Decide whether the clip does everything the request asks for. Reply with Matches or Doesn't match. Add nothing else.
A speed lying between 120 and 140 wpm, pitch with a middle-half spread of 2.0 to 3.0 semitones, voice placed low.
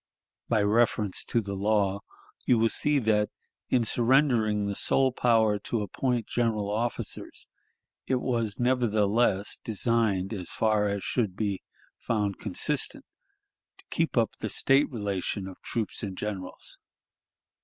Matches